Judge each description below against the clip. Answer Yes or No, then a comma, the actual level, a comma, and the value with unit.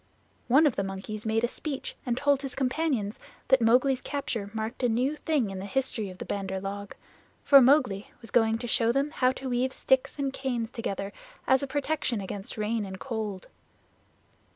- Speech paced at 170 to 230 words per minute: Yes, average, 190 wpm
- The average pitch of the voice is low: No, high, 240 Hz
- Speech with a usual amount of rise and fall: Yes, average, 4.2 semitones